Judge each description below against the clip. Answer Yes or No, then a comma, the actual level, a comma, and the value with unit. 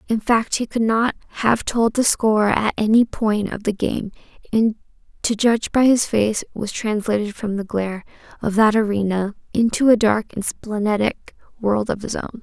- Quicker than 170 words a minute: Yes, average, 185 wpm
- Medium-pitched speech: No, high, 215 Hz